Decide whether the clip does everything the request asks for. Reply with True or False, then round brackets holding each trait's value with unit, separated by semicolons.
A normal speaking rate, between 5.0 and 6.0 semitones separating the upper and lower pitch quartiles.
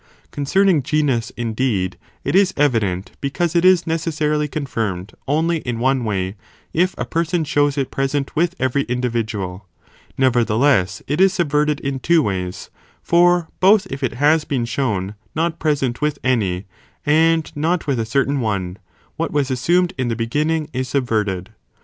True (155 wpm; 5.6 semitones)